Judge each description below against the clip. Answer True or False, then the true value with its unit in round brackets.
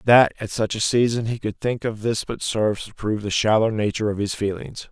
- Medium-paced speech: False (245 wpm)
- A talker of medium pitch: False (110 Hz)